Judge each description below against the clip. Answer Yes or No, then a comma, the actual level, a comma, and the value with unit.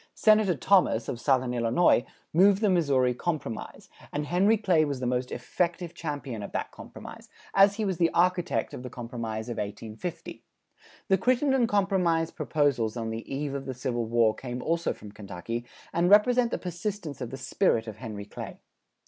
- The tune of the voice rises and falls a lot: Yes, wide, 7.4 semitones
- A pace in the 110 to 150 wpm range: No, average, 175 wpm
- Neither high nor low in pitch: Yes, medium, 145 Hz